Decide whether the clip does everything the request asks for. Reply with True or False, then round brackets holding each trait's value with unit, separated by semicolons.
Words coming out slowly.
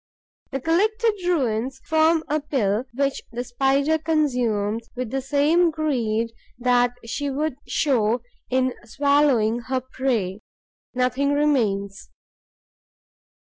True (105 wpm)